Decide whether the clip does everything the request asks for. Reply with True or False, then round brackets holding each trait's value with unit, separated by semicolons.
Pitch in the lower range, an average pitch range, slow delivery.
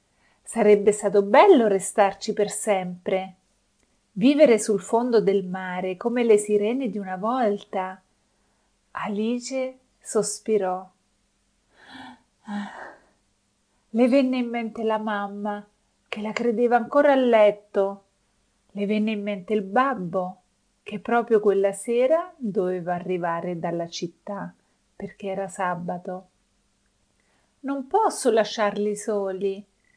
False (205 Hz; 3.0 semitones; 105 wpm)